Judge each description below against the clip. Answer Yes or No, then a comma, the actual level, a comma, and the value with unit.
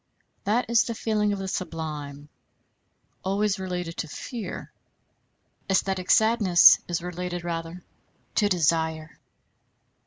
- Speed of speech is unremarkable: No, slow, 105 wpm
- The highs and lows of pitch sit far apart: No, average, 3.7 semitones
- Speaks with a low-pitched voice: No, medium, 180 Hz